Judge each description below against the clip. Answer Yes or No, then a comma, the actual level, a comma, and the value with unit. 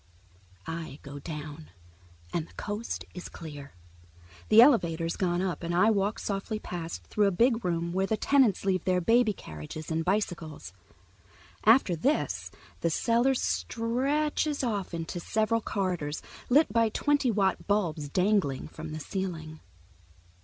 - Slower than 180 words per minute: Yes, average, 145 wpm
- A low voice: No, high, 190 Hz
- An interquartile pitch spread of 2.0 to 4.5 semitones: No, wide, 5.5 semitones